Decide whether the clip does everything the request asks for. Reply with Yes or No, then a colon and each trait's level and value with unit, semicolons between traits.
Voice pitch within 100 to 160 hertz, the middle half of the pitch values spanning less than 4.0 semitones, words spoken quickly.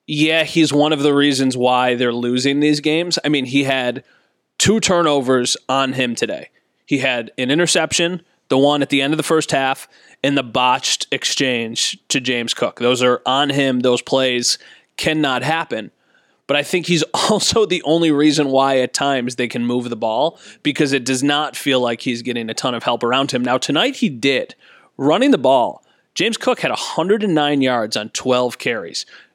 No: low, 135 Hz; average, 3.3 semitones; average, 190 wpm